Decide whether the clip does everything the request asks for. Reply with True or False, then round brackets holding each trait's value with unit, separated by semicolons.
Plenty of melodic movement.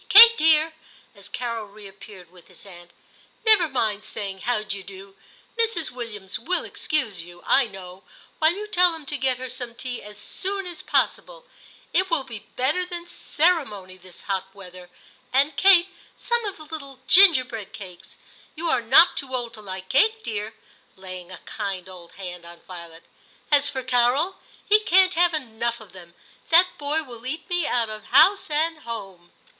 True (8.9 semitones)